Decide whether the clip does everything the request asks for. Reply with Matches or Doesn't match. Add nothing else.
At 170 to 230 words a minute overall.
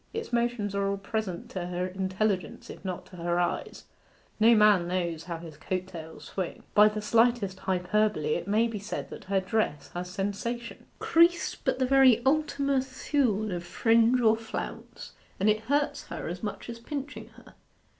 Matches